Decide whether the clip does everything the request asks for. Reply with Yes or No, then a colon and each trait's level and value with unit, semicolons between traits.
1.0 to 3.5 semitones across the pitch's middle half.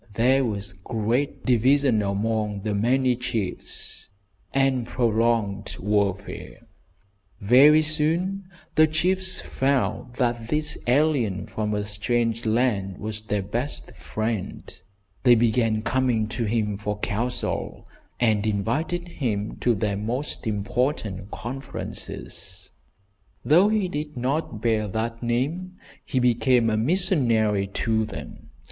No: average, 4.1 semitones